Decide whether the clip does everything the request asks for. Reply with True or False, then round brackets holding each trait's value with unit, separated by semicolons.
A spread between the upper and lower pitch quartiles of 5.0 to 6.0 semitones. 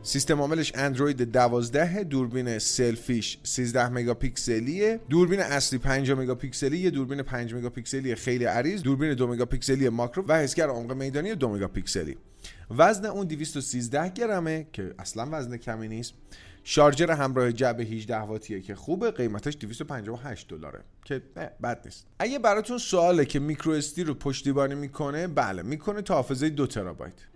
False (4.3 semitones)